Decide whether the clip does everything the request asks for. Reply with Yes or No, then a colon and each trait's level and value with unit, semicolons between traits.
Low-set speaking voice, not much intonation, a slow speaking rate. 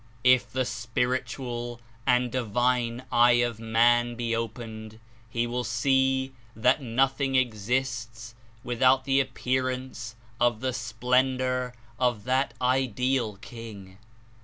Yes: low, 120 Hz; narrow, 1.9 semitones; slow, 110 wpm